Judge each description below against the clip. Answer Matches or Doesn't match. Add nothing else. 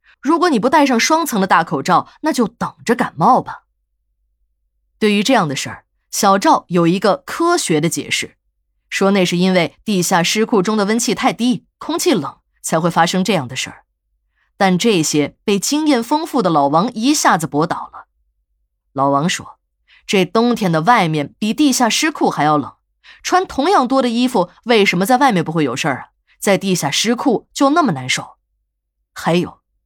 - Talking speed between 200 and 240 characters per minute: Doesn't match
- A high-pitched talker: Matches